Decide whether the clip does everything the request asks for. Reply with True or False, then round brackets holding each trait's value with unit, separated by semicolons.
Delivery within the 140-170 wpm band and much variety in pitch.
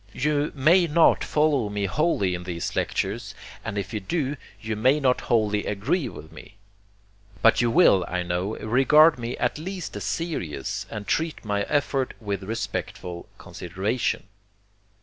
True (150 wpm; 7.1 semitones)